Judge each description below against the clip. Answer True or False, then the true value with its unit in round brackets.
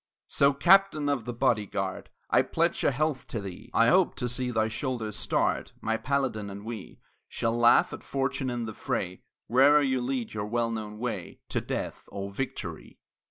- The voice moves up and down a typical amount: True (3.9 semitones)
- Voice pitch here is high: False (120 Hz)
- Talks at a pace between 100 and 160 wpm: False (185 wpm)